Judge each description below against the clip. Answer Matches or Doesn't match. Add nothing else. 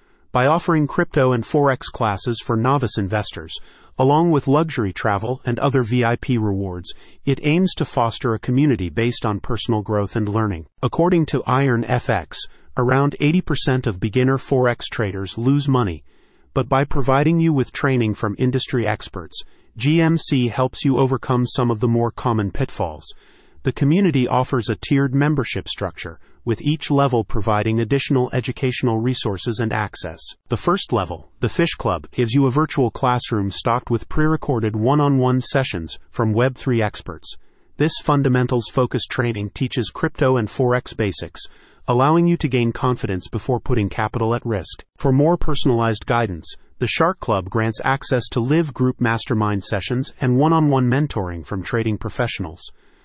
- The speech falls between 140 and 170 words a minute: Matches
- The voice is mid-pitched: Doesn't match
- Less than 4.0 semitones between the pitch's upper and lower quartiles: Matches